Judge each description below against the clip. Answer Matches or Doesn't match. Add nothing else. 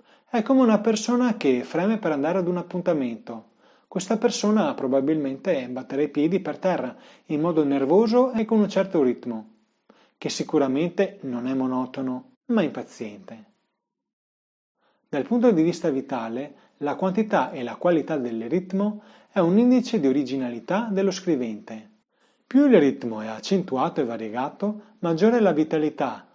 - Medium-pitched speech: Matches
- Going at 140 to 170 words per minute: Matches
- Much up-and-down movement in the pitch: Matches